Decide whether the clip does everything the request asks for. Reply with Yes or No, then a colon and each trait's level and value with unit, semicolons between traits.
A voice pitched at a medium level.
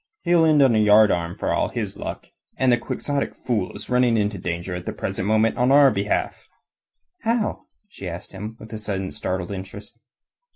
No: low, 110 Hz